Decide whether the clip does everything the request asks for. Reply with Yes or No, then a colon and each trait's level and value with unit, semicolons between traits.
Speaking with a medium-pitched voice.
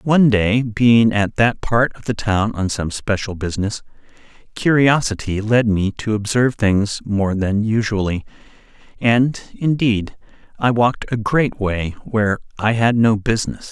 No: low, 110 Hz